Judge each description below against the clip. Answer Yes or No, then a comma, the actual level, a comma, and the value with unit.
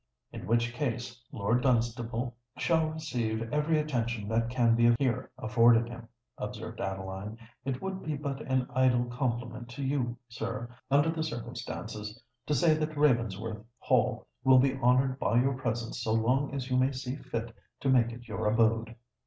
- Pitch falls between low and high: No, low, 120 Hz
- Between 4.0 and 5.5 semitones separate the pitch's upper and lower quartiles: No, narrow, 2.6 semitones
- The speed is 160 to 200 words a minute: Yes, average, 165 wpm